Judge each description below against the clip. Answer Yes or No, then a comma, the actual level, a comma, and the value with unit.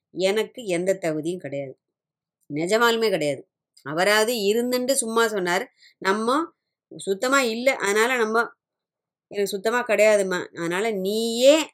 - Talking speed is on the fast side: No, average, 100 wpm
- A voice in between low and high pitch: No, high, 215 Hz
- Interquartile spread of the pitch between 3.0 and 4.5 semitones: Yes, average, 4.0 semitones